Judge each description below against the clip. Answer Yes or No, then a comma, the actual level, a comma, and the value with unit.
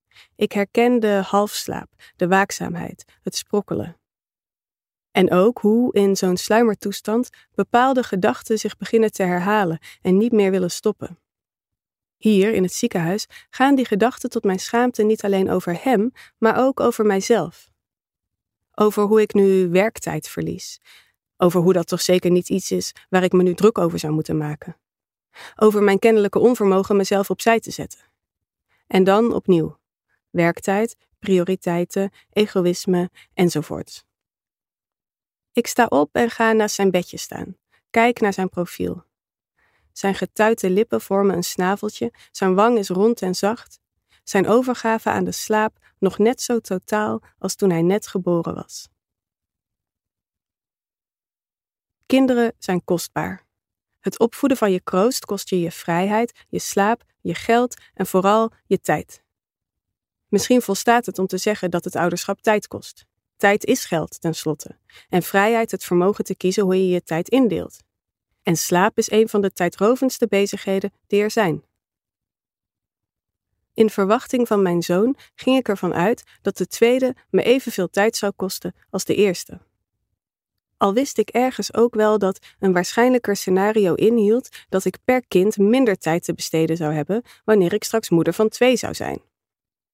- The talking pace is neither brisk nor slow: Yes, average, 150 wpm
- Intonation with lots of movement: No, average, 3.7 semitones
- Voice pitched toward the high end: Yes, high, 200 Hz